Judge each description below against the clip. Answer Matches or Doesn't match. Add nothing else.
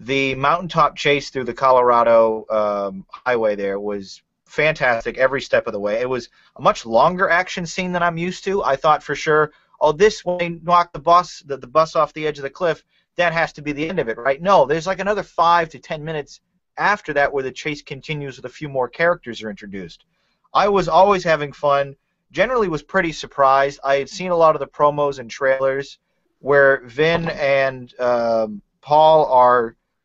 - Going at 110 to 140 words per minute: Doesn't match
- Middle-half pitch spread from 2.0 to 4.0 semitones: Doesn't match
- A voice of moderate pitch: Matches